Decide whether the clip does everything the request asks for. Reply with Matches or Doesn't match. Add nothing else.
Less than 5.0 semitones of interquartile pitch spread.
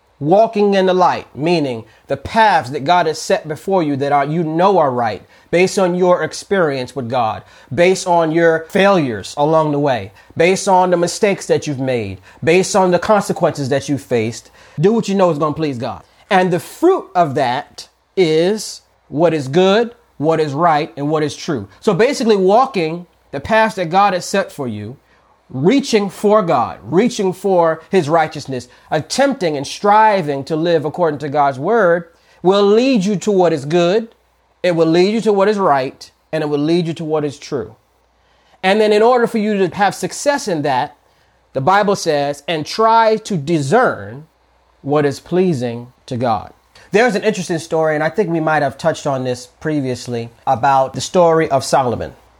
Doesn't match